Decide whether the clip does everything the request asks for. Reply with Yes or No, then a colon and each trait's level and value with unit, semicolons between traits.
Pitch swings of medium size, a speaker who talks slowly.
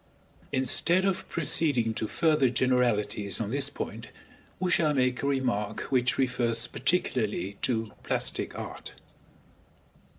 Yes: average, 4.1 semitones; slow, 120 wpm